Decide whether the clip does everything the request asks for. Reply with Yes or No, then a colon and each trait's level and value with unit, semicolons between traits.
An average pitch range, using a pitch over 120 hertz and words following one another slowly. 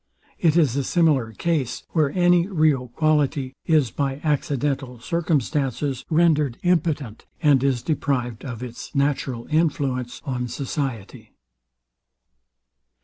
Yes: average, 3.6 semitones; medium, 140 Hz; slow, 110 wpm